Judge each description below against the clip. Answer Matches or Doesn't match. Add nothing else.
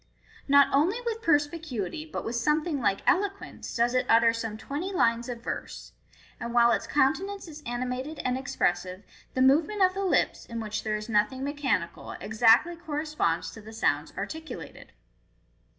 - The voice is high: Matches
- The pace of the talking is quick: Doesn't match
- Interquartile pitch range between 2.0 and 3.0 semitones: Doesn't match